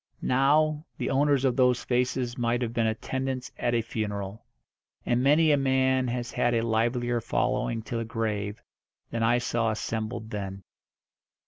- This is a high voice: No, low, 120 Hz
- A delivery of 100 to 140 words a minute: No, average, 155 wpm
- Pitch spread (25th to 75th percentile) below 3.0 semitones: Yes, narrow, 2.6 semitones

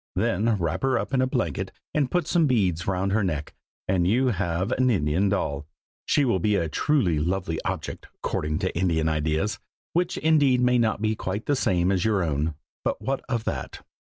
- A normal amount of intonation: No, wide, 7.0 semitones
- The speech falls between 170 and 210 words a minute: Yes, average, 195 wpm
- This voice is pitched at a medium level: No, very low, 95 Hz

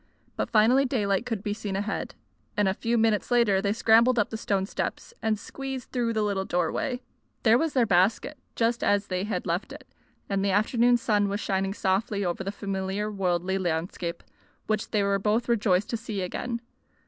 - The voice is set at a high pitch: Yes, high, 210 Hz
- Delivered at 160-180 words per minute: No, average, 190 wpm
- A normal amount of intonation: Yes, average, 3.1 semitones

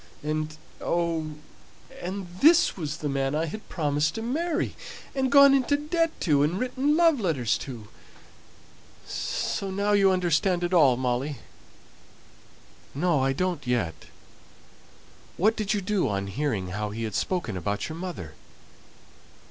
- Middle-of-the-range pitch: Yes, medium, 170 Hz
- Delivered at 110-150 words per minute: Yes, average, 140 wpm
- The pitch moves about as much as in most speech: No, wide, 7.5 semitones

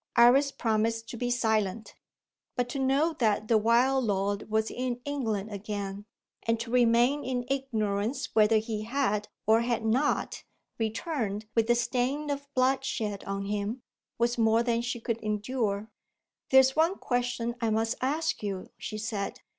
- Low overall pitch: No, high, 230 Hz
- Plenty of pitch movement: No, average, 3.1 semitones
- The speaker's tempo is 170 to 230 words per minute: No, average, 155 wpm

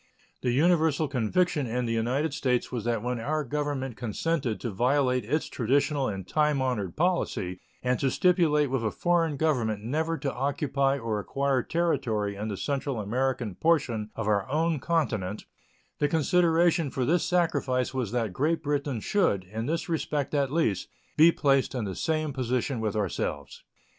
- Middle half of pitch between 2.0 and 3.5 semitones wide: No, average, 5.1 semitones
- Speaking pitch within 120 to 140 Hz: Yes, low, 135 Hz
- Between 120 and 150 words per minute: No, average, 165 wpm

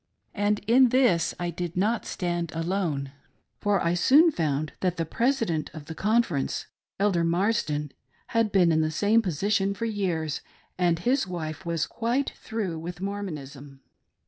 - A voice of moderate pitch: Yes, medium, 180 Hz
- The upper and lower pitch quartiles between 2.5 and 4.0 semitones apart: No, average, 4.5 semitones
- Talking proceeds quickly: No, average, 160 wpm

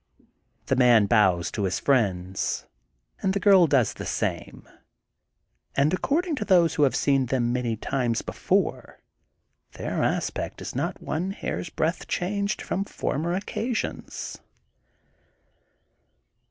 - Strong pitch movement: Yes, wide, 8.3 semitones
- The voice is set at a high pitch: No, medium, 140 Hz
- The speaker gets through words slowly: Yes, slow, 125 wpm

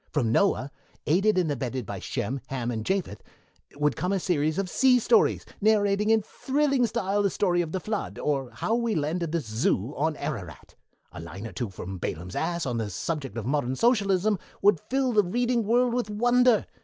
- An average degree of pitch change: No, wide, 8.5 semitones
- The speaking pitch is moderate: Yes, medium, 175 Hz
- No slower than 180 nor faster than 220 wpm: Yes, average, 190 wpm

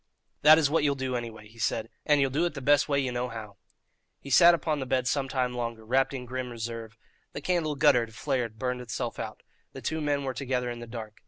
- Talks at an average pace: No, fast, 245 wpm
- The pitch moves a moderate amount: Yes, average, 3.3 semitones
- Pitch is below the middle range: Yes, low, 125 Hz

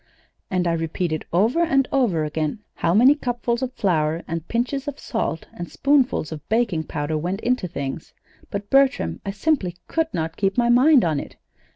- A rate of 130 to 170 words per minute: No, average, 180 wpm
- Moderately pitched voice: No, high, 195 Hz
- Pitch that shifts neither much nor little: No, wide, 7.7 semitones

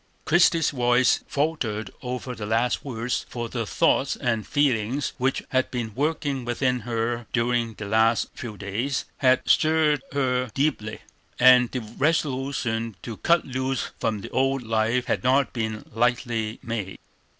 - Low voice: Yes, low, 125 Hz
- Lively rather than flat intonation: No, average, 2.9 semitones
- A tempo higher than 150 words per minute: No, average, 145 wpm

